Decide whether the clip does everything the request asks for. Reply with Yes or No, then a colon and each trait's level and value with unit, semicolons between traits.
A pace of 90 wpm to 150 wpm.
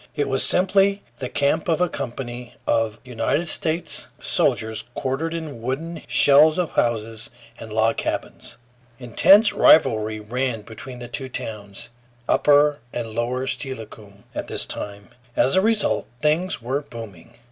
Yes: average, 140 wpm